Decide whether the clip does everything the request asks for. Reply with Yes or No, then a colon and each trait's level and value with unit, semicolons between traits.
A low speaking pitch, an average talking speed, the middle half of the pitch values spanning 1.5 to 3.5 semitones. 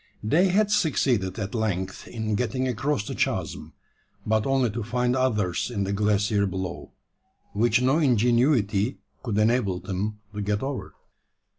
No: low, 110 Hz; average, 145 wpm; average, 3.9 semitones